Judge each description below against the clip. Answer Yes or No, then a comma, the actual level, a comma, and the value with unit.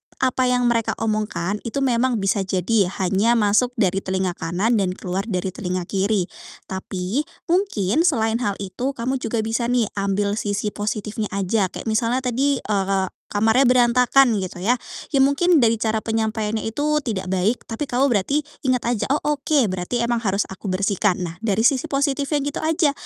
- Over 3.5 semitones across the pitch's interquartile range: Yes, average, 4.3 semitones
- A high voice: Yes, high, 225 Hz